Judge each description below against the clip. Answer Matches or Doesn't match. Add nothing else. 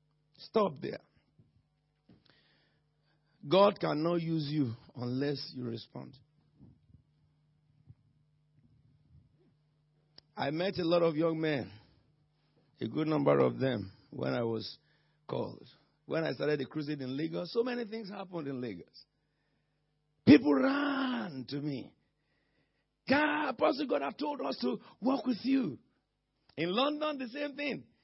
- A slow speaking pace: Matches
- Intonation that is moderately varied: Matches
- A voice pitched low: Doesn't match